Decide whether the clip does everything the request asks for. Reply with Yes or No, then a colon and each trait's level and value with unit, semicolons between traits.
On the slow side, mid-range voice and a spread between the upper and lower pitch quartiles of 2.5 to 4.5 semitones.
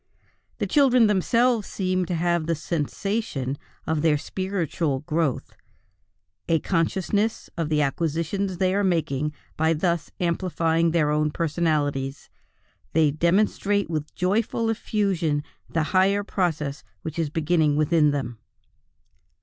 Yes: slow, 120 wpm; medium, 165 Hz; average, 3.9 semitones